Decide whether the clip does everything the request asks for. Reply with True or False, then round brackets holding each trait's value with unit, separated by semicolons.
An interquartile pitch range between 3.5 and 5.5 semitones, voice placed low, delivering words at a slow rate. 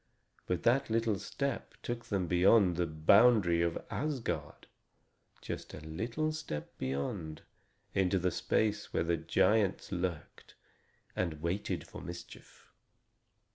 True (5.2 semitones; 90 Hz; 120 wpm)